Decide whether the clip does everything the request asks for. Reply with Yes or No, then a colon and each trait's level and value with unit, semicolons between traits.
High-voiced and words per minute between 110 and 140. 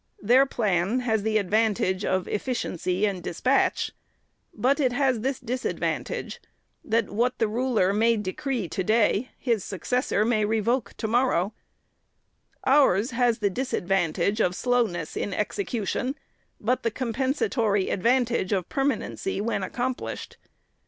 Yes: high, 225 Hz; slow, 135 wpm